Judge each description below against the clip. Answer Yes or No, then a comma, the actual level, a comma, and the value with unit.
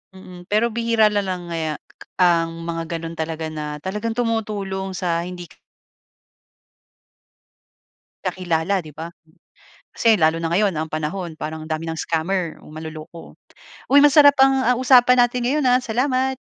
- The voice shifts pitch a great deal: Yes, wide, 6.0 semitones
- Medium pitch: Yes, medium, 180 Hz